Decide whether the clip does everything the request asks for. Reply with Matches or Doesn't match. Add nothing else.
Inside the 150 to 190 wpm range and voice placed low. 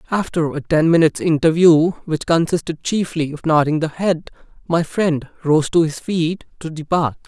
Doesn't match